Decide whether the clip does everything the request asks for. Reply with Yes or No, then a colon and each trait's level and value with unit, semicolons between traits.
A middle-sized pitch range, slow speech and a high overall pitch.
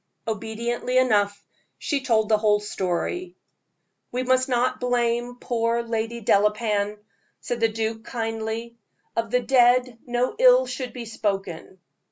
No: narrow, 2.3 semitones; slow, 130 wpm; high, 230 Hz